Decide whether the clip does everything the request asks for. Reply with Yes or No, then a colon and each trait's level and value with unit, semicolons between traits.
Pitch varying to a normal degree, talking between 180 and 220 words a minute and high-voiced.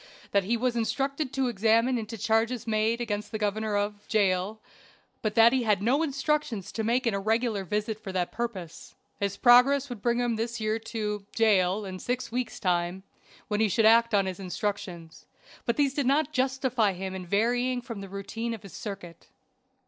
Yes: average, 3.3 semitones; average, 185 wpm; high, 220 Hz